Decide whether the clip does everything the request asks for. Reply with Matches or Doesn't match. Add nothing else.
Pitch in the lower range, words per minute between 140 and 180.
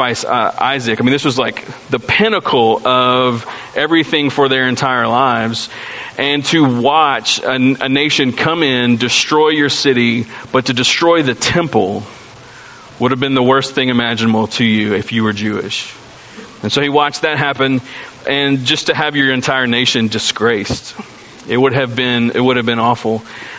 Matches